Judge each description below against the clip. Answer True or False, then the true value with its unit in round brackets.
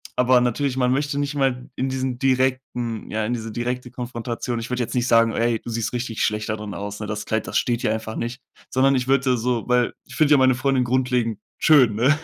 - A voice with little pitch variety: True (2.2 semitones)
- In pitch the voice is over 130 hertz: False (125 Hz)